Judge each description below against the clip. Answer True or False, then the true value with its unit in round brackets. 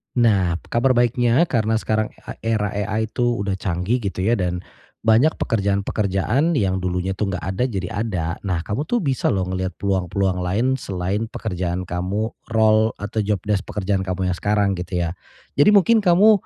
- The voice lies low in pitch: True (100 Hz)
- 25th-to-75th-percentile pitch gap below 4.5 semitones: True (3.6 semitones)